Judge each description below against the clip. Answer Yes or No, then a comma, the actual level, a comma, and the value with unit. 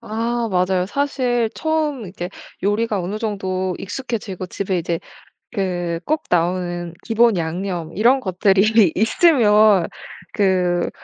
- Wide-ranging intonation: No, average, 4.2 semitones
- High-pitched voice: Yes, high, 200 Hz